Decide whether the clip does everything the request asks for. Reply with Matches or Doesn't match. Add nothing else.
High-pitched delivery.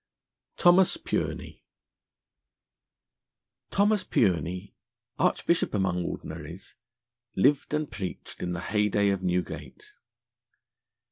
Doesn't match